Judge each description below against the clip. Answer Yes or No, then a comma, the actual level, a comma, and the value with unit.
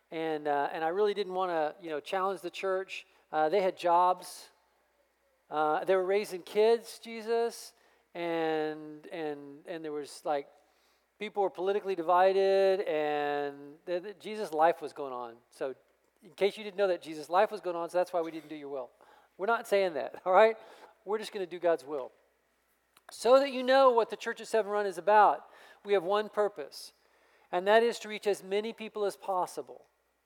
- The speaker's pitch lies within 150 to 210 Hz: Yes, high, 190 Hz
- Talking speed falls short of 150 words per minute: No, average, 200 wpm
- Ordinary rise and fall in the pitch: Yes, average, 4.7 semitones